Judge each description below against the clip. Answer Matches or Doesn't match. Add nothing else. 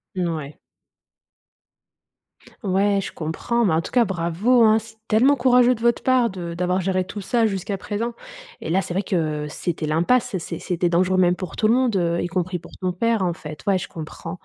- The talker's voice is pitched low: Doesn't match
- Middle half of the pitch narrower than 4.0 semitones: Doesn't match